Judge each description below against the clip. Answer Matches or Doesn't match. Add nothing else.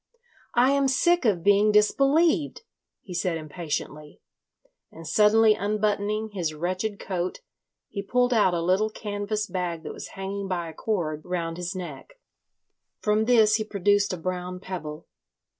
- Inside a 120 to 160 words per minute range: Matches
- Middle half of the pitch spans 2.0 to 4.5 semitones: Matches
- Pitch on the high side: Matches